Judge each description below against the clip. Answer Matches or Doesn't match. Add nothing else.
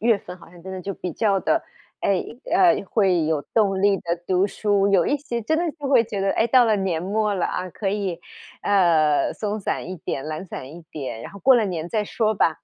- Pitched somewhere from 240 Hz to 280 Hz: Doesn't match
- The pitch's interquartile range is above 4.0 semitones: Doesn't match